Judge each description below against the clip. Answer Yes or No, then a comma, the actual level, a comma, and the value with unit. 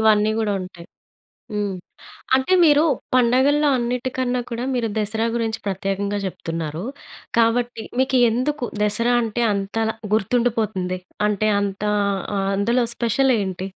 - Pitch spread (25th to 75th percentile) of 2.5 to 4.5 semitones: Yes, average, 3.5 semitones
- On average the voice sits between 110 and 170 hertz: No, high, 225 Hz